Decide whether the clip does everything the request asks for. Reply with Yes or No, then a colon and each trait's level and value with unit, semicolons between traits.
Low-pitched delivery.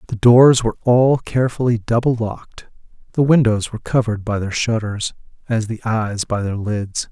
Yes: low, 115 Hz